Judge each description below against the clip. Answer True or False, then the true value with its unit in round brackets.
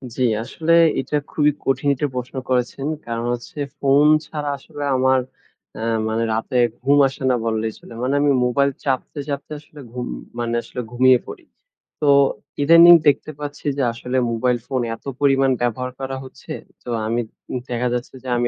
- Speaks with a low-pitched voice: True (130 Hz)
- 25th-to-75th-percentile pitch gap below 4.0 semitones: True (2.8 semitones)